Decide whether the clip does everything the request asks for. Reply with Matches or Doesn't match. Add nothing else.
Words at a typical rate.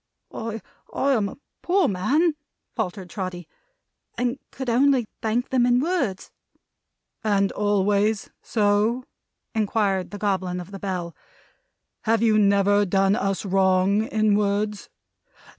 Doesn't match